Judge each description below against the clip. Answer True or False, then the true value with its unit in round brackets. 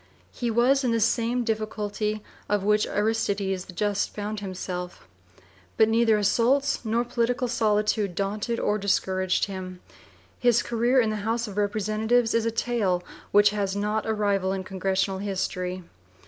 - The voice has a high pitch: True (210 Hz)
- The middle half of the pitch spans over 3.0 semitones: False (2.7 semitones)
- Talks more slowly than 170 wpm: True (160 wpm)